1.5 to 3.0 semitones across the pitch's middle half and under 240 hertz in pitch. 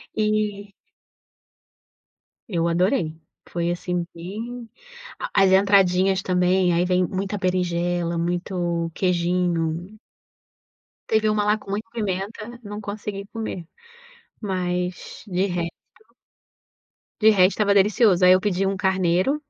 Yes: average, 2.7 semitones; high, 190 Hz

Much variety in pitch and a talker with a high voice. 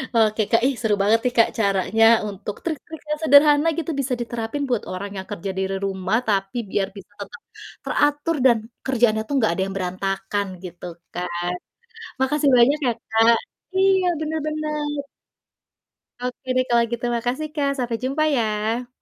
Yes: wide, 6.0 semitones; high, 235 Hz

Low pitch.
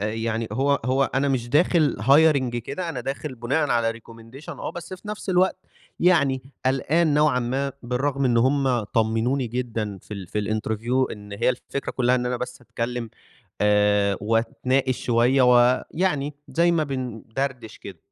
Yes: low, 125 Hz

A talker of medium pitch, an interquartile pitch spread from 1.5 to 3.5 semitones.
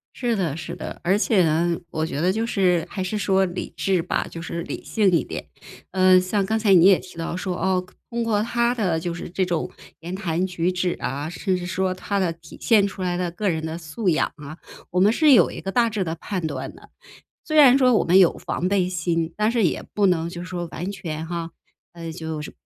Yes: medium, 180 Hz; average, 2.9 semitones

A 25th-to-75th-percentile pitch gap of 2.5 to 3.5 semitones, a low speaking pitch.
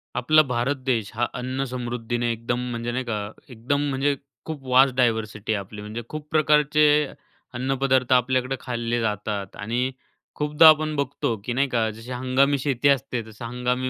Yes: average, 2.8 semitones; low, 125 Hz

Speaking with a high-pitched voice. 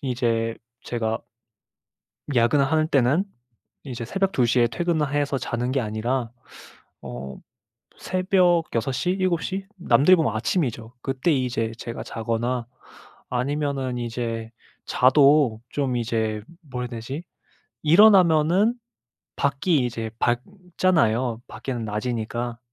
No: low, 125 Hz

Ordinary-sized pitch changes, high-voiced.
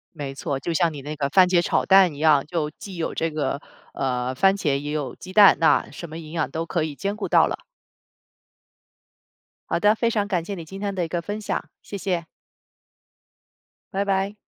No: average, 4.4 semitones; medium, 170 Hz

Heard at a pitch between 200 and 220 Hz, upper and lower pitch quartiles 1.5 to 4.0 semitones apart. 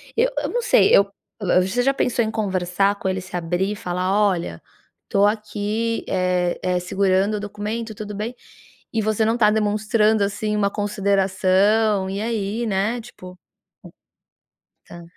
Yes: high, 205 Hz; narrow, 2.5 semitones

